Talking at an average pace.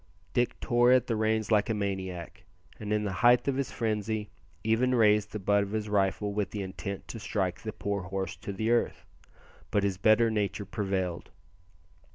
Yes: average, 190 wpm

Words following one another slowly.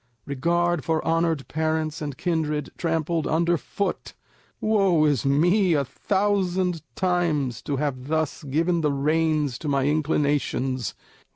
Yes: slow, 125 wpm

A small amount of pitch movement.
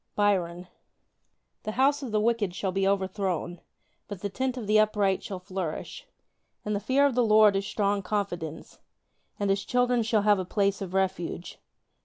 Yes: narrow, 2.3 semitones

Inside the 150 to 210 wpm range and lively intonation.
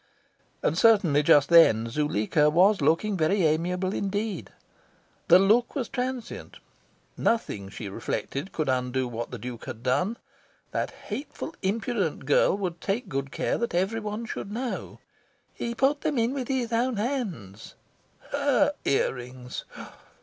No: average, 140 wpm; wide, 8.7 semitones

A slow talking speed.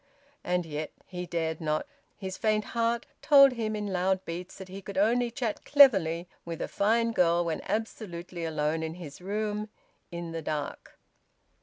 No: average, 165 wpm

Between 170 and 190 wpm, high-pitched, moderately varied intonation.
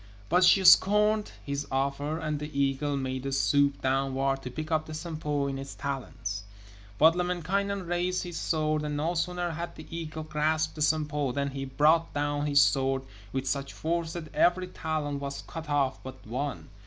No: average, 180 wpm; medium, 150 Hz; average, 3.1 semitones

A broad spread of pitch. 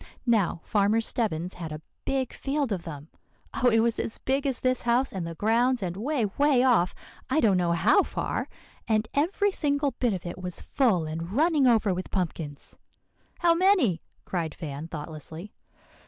Yes: wide, 7.2 semitones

